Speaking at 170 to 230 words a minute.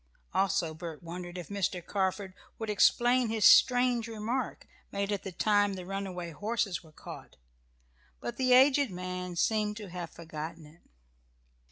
No: average, 150 wpm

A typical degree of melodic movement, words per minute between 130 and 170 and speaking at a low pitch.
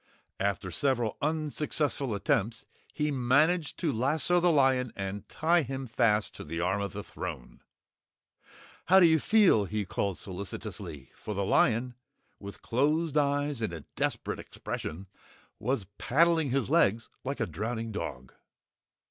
No: wide, 6.7 semitones; average, 140 wpm; low, 120 Hz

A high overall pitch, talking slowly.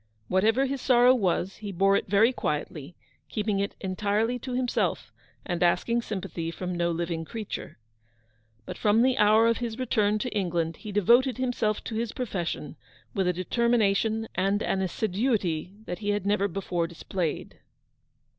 No: high, 205 Hz; average, 165 wpm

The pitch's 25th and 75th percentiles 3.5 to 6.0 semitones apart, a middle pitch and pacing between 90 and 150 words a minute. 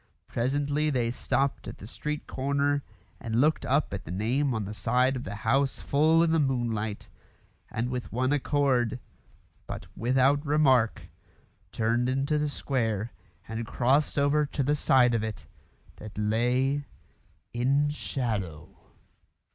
No: average, 3.8 semitones; low, 130 Hz; average, 140 wpm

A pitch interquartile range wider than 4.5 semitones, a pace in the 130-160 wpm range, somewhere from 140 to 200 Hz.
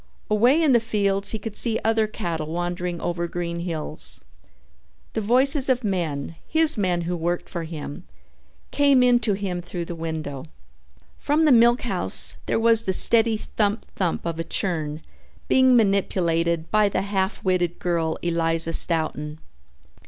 Yes: average, 5.1 semitones; average, 150 wpm; medium, 185 Hz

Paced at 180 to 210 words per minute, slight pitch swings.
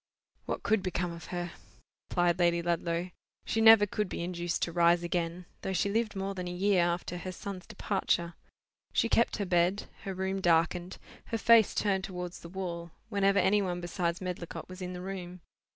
Yes: average, 185 wpm; narrow, 2.1 semitones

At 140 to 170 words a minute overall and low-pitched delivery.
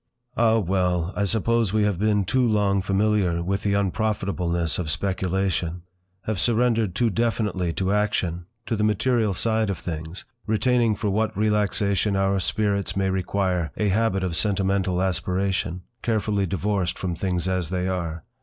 Yes: average, 150 wpm; low, 100 Hz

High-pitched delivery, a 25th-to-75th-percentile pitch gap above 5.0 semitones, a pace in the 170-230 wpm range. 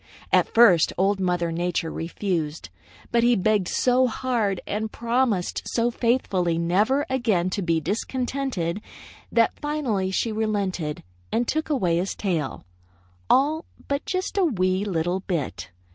No: high, 205 Hz; wide, 5.6 semitones; slow, 135 wpm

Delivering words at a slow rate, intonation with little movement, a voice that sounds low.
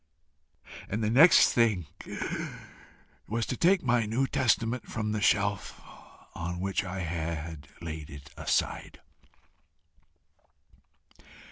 No: slow, 105 wpm; wide, 5.6 semitones; low, 105 Hz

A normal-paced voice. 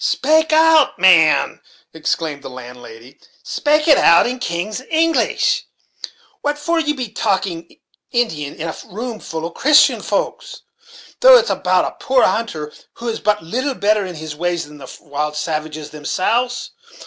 Yes: average, 165 wpm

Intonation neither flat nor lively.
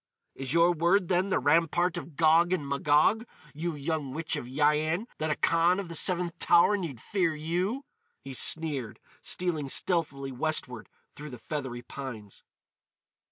Yes: average, 3.7 semitones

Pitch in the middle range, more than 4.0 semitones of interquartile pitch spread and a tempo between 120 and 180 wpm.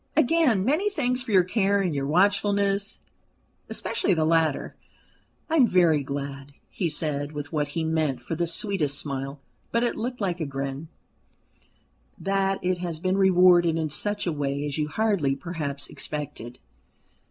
Yes: medium, 170 Hz; wide, 5.4 semitones; average, 160 wpm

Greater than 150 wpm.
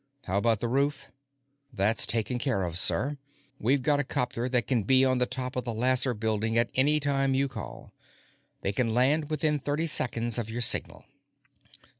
Yes: average, 180 wpm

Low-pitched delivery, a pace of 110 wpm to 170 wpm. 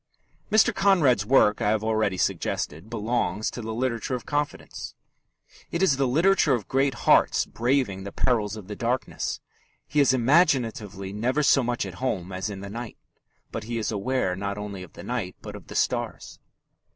No: low, 115 Hz; average, 180 wpm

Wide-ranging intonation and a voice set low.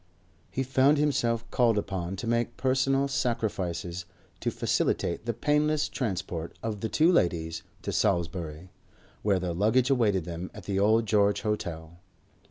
Yes: wide, 6.2 semitones; low, 105 Hz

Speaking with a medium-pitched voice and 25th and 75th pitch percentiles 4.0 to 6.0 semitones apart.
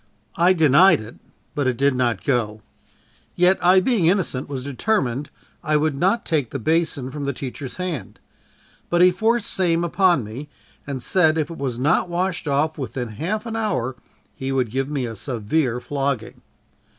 Yes: medium, 145 Hz; wide, 5.5 semitones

